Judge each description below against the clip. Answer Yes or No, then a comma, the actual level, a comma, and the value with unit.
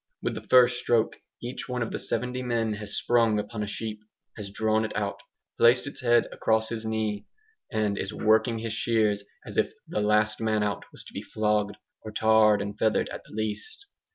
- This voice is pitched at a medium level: No, low, 110 Hz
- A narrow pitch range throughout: Yes, narrow, 1.5 semitones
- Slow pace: No, average, 200 wpm